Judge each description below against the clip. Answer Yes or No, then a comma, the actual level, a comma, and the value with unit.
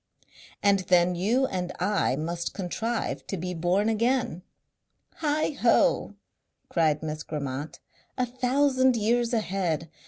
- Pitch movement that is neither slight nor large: No, wide, 6.1 semitones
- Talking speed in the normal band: No, slow, 115 wpm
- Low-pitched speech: No, high, 195 Hz